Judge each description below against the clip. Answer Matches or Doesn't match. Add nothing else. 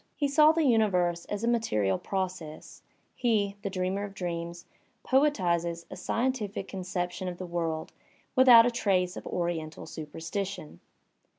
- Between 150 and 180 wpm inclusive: Doesn't match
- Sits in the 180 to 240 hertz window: Matches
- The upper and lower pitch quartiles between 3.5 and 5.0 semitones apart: Matches